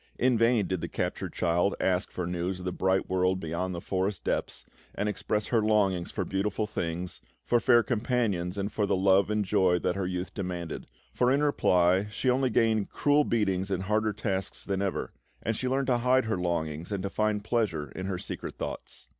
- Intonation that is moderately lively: Yes, average, 3.2 semitones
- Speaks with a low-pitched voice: Yes, low, 100 Hz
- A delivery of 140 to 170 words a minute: No, fast, 205 wpm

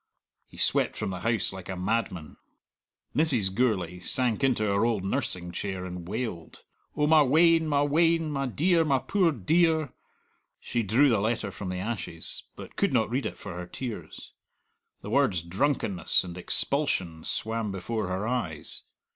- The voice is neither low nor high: No, low, 110 Hz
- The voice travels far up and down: Yes, wide, 7.5 semitones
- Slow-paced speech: No, average, 165 wpm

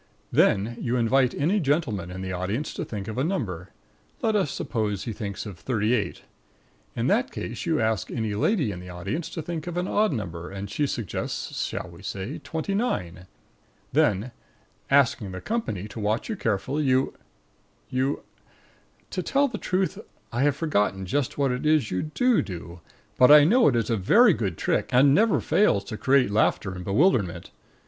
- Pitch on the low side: Yes, low, 120 Hz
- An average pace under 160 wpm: No, average, 185 wpm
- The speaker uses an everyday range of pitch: No, wide, 7.6 semitones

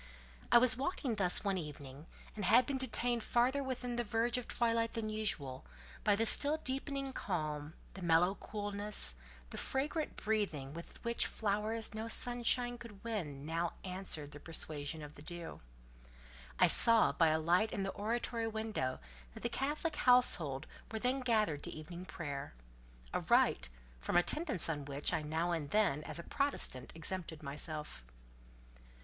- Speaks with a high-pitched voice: Yes, high, 200 Hz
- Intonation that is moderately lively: No, wide, 7.3 semitones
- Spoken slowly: No, average, 155 wpm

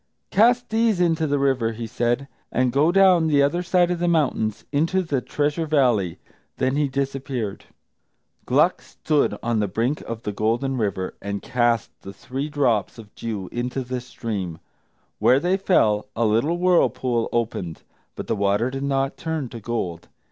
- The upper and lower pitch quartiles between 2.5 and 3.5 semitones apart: No, average, 5.2 semitones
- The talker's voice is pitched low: Yes, low, 130 Hz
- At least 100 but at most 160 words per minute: No, average, 170 wpm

